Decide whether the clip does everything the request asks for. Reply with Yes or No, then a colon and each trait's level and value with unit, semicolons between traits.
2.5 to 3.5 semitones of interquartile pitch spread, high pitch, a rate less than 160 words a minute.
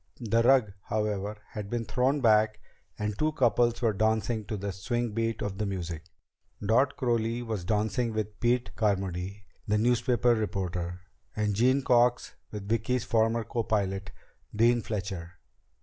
No: average, 2.8 semitones; low, 110 Hz; average, 145 wpm